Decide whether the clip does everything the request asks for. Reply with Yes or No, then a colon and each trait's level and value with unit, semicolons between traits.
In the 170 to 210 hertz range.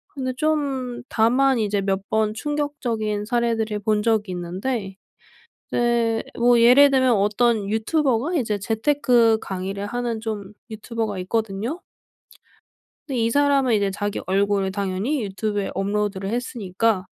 No: high, 220 Hz